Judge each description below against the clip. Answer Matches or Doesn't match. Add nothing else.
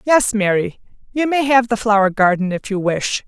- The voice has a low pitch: Doesn't match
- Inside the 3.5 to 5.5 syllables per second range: Matches